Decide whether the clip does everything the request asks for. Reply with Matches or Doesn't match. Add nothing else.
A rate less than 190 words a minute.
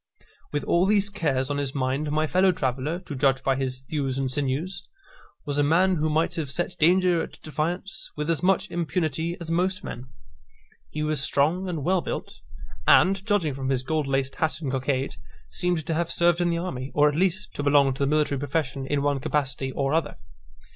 Doesn't match